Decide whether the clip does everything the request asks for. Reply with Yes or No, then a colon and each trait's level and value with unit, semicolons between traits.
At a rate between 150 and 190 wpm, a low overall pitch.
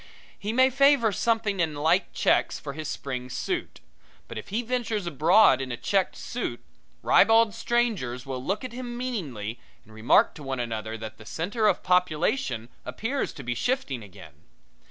No: average, 170 wpm; medium, 175 Hz